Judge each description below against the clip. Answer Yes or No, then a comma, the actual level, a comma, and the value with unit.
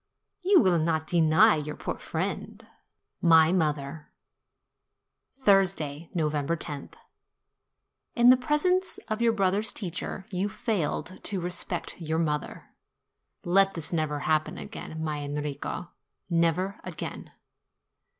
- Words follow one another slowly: Yes, slow, 115 wpm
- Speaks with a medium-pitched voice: Yes, medium, 170 Hz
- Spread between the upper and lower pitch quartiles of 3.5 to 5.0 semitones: Yes, average, 4.3 semitones